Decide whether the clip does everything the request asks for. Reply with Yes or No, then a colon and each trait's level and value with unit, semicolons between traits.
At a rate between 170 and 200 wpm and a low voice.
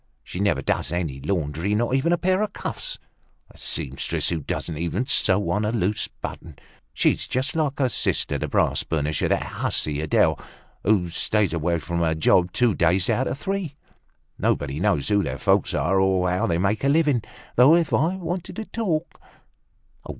Yes: average, 180 wpm; low, 100 Hz